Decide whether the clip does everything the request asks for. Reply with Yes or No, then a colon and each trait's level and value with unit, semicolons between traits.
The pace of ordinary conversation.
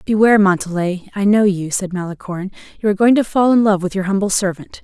No: fast, 225 wpm